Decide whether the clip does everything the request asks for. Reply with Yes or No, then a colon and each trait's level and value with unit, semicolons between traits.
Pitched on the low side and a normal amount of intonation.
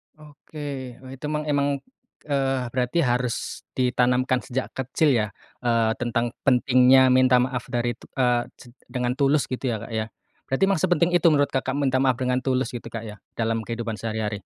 No: low, 125 Hz; narrow, 2.2 semitones